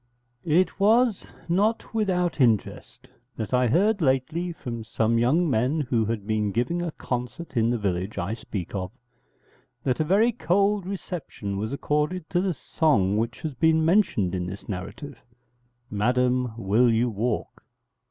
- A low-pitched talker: Yes, low, 125 Hz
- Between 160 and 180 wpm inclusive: No, average, 150 wpm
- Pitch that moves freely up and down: Yes, wide, 7.8 semitones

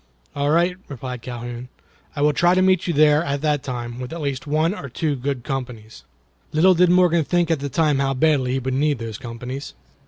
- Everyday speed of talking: No, fast, 215 wpm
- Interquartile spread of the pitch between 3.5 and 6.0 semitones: Yes, average, 4.0 semitones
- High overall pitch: No, medium, 140 Hz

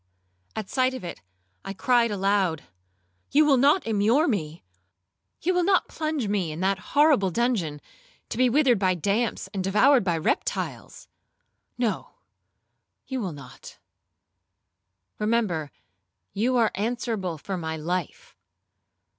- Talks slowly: Yes, slow, 125 wpm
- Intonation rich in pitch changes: Yes, wide, 6.1 semitones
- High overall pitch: Yes, high, 210 Hz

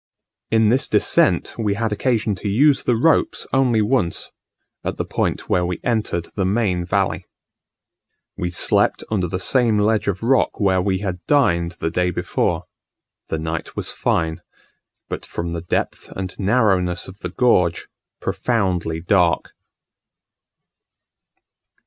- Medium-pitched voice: No, very low, 95 Hz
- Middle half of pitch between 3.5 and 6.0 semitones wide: Yes, average, 4.3 semitones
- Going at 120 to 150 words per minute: Yes, average, 140 wpm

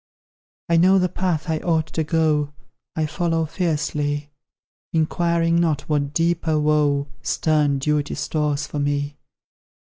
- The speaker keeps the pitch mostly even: Yes, narrow, 2.1 semitones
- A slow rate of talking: Yes, slow, 125 wpm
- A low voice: No, medium, 155 Hz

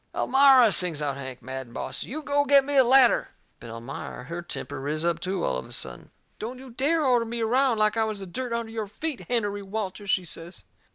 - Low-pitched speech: No, high, 215 Hz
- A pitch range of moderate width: No, wide, 7.5 semitones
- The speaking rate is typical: No, fast, 230 wpm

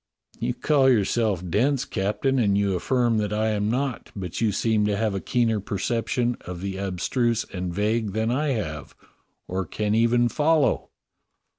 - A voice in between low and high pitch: No, low, 110 Hz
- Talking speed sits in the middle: Yes, average, 165 wpm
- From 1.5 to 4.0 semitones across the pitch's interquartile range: Yes, average, 3.6 semitones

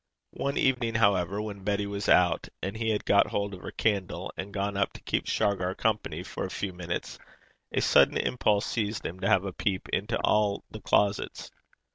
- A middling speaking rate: Yes, average, 195 wpm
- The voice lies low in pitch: Yes, low, 100 Hz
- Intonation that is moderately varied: No, narrow, 1.8 semitones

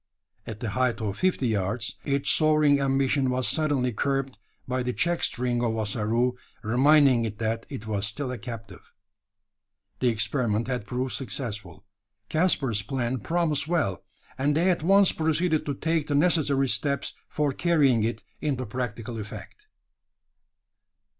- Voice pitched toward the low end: Yes, low, 130 Hz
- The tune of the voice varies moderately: Yes, average, 4.5 semitones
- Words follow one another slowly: No, average, 145 wpm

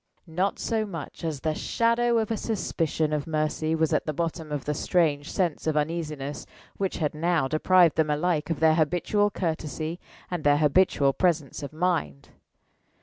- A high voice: No, medium, 160 Hz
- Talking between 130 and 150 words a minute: No, average, 170 wpm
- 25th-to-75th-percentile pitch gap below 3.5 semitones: Yes, average, 3.0 semitones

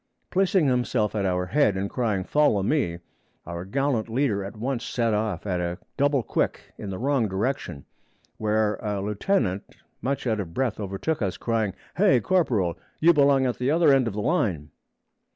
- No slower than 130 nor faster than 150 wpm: No, average, 175 wpm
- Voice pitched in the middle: No, low, 110 Hz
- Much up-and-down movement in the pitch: Yes, wide, 5.9 semitones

